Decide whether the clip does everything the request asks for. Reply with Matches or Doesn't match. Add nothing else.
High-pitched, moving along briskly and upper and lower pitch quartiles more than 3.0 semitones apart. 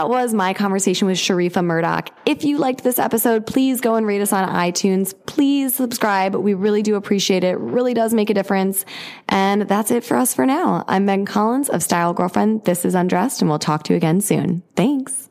Matches